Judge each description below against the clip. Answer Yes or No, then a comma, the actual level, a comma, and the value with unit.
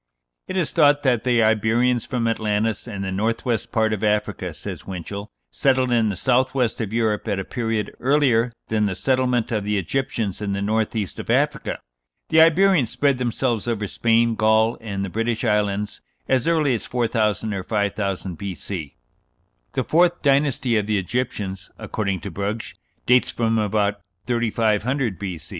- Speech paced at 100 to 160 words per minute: No, average, 170 wpm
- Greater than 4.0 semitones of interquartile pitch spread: No, average, 3.4 semitones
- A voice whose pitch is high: No, low, 110 Hz